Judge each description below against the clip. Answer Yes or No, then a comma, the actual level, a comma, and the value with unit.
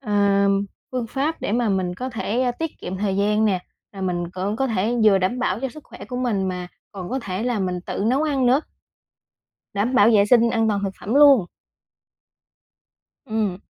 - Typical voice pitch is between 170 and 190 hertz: No, high, 215 Hz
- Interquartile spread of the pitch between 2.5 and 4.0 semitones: No, average, 4.6 semitones